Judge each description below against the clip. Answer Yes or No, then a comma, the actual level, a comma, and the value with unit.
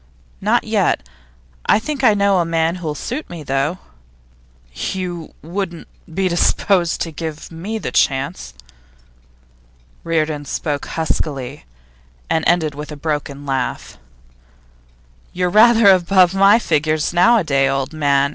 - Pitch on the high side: No, medium, 165 Hz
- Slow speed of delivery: Yes, slow, 125 wpm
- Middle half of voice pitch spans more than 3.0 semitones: Yes, average, 4.1 semitones